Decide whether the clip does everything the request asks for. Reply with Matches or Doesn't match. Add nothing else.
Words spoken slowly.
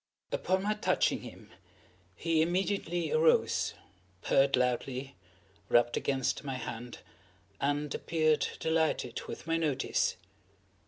Matches